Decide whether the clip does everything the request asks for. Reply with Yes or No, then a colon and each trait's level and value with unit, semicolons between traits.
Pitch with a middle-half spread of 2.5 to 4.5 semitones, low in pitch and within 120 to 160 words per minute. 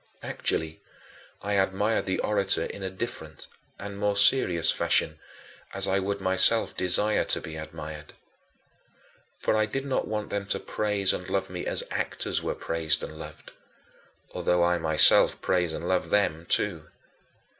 Yes: average, 3.7 semitones; very low, 95 Hz; average, 155 wpm